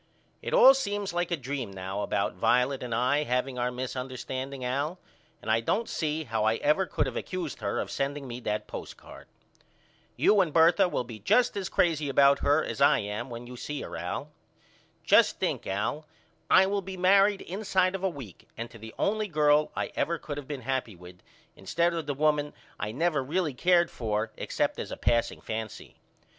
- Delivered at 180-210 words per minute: Yes, average, 195 wpm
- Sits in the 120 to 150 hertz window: Yes, medium, 140 Hz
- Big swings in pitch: Yes, wide, 6.2 semitones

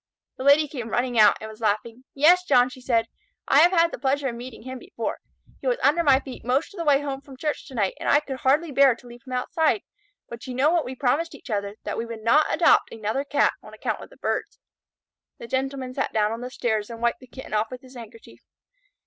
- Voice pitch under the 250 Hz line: No, very high, 260 Hz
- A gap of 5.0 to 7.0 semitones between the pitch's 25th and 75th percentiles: No, average, 3.5 semitones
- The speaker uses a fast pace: Yes, fast, 250 wpm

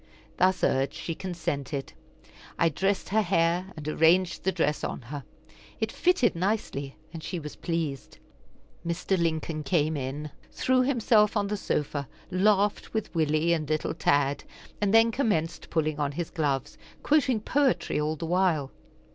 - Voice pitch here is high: No, medium, 165 Hz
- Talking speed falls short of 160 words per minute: Yes, average, 150 wpm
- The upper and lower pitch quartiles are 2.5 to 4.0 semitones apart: No, average, 4.8 semitones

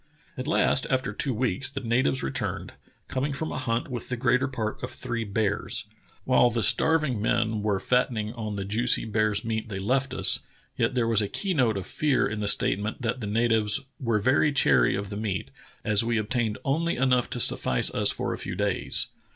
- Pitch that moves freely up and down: No, average, 3.5 semitones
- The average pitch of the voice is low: Yes, low, 115 Hz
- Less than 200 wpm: No, fast, 205 wpm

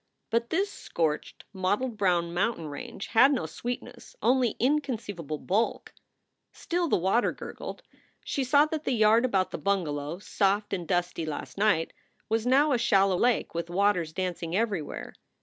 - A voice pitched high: Yes, high, 200 Hz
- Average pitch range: No, wide, 5.9 semitones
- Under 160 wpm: Yes, average, 150 wpm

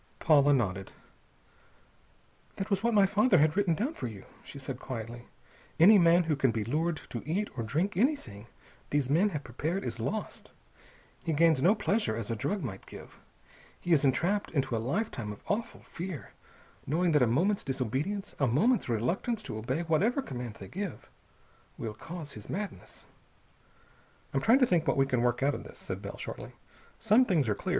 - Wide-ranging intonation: Yes, wide, 8.2 semitones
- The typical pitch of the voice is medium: Yes, medium, 155 Hz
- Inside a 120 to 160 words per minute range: No, average, 185 wpm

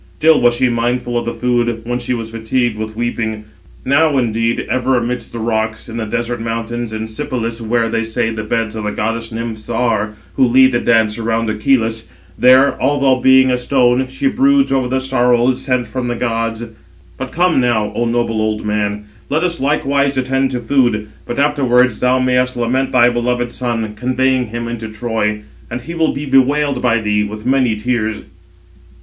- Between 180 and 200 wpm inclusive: Yes, average, 185 wpm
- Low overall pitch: Yes, low, 120 Hz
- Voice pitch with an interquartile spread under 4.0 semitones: Yes, narrow, 2.4 semitones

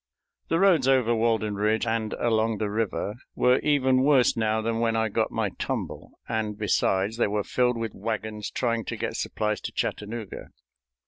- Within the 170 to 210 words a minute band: Yes, average, 175 wpm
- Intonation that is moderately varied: No, narrow, 1.9 semitones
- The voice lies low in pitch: Yes, low, 110 Hz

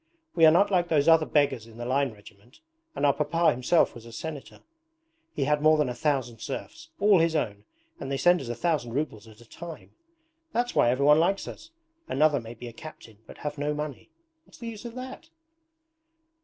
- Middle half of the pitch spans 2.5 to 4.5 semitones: No, wide, 5.4 semitones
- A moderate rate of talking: No, fast, 210 wpm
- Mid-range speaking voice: Yes, medium, 150 Hz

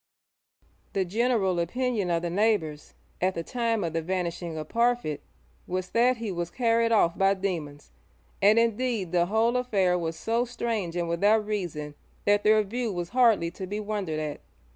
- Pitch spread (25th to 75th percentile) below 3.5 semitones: No, average, 4.9 semitones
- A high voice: Yes, high, 195 Hz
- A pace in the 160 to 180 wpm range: Yes, average, 170 wpm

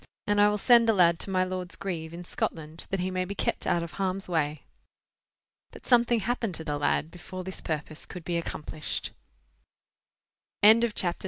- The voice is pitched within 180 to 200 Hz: Yes, medium, 185 Hz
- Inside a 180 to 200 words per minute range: Yes, average, 185 wpm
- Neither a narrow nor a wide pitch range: Yes, average, 3.3 semitones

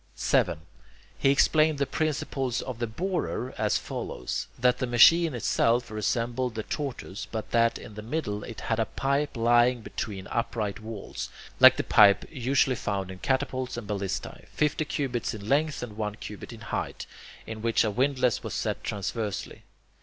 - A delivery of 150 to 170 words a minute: Yes, average, 165 wpm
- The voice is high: No, low, 120 Hz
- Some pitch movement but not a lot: Yes, average, 3.9 semitones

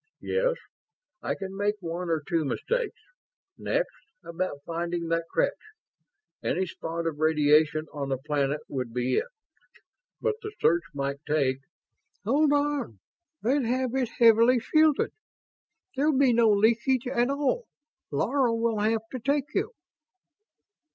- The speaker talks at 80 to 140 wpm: Yes, slow, 135 wpm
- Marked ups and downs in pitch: Yes, wide, 9.0 semitones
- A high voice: Yes, high, 215 Hz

